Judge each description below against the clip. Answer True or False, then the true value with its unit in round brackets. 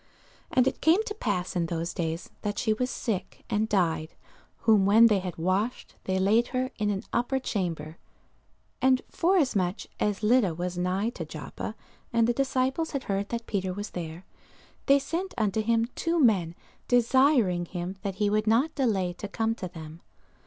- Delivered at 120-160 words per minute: False (175 wpm)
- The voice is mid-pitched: False (210 Hz)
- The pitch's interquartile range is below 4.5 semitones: False (5.4 semitones)